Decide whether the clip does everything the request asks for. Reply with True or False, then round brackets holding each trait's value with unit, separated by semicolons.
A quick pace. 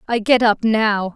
True (210 wpm)